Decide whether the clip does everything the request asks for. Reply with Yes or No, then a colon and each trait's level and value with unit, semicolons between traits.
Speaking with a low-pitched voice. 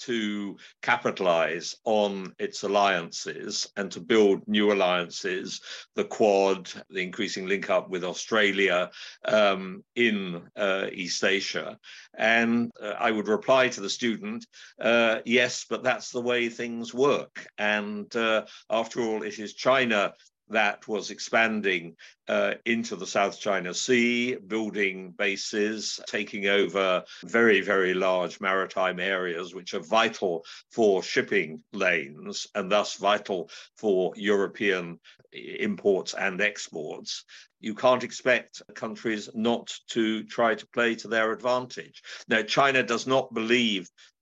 Yes: low, 110 Hz